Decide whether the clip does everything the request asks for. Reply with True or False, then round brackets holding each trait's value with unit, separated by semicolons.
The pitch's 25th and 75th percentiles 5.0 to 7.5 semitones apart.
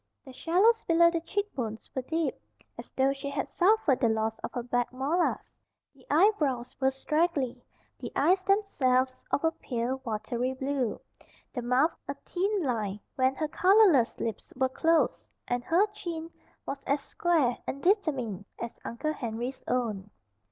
True (5.4 semitones)